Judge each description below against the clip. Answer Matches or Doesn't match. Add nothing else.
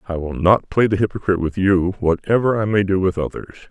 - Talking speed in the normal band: Doesn't match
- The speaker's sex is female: Doesn't match